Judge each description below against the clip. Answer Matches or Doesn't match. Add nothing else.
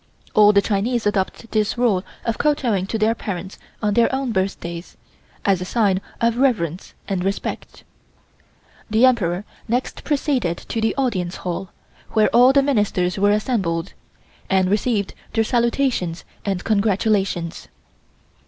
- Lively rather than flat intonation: Doesn't match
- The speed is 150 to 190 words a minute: Doesn't match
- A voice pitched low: Doesn't match